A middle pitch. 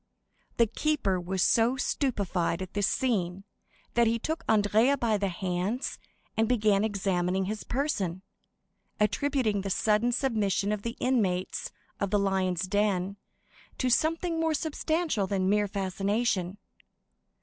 No: high, 205 Hz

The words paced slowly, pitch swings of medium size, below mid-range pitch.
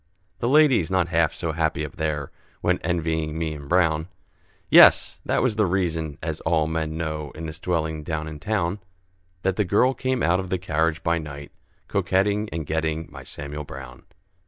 No: average, 180 wpm; average, 3.1 semitones; very low, 80 Hz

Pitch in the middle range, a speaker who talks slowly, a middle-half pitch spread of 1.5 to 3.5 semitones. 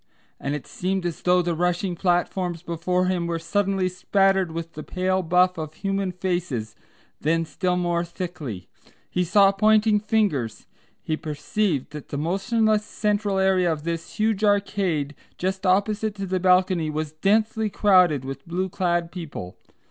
No: medium, 180 Hz; average, 155 wpm; average, 3.0 semitones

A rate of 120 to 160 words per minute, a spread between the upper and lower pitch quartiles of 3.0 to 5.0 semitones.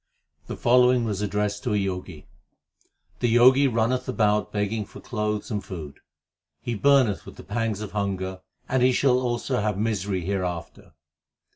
Yes: average, 155 wpm; average, 3.5 semitones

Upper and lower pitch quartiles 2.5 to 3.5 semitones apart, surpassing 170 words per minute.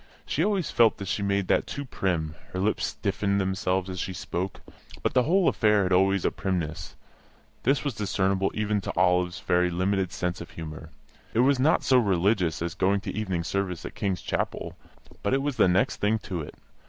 Yes: average, 3.0 semitones; average, 200 wpm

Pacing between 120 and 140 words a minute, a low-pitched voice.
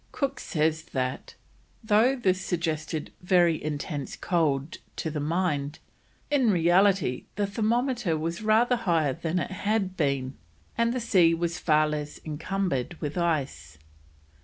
No: slow, 135 wpm; medium, 170 Hz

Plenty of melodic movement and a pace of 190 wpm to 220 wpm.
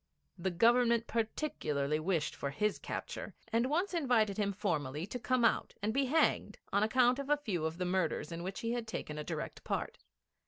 Yes: wide, 6.4 semitones; average, 195 wpm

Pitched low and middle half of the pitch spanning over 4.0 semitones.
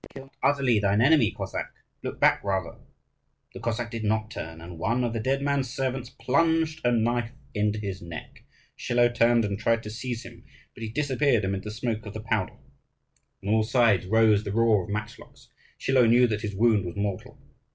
No: low, 115 Hz; average, 2.8 semitones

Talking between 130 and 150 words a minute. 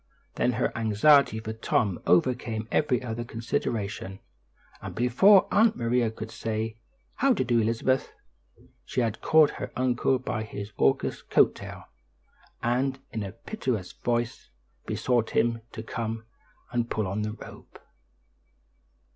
Yes: average, 140 wpm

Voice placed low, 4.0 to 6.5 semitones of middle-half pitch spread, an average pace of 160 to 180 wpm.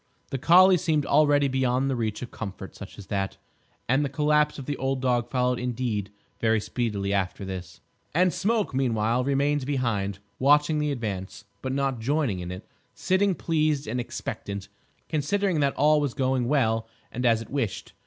Yes: low, 130 Hz; average, 4.8 semitones; average, 175 wpm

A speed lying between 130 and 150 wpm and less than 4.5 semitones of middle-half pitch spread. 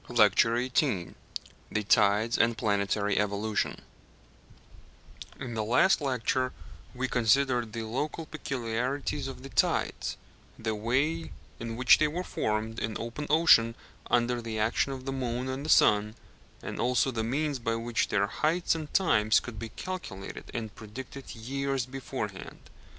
Yes: average, 145 wpm; average, 3.6 semitones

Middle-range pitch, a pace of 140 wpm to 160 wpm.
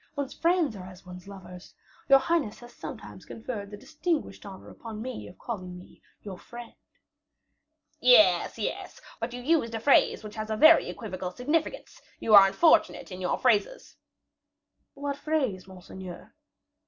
No: high, 220 Hz; average, 155 wpm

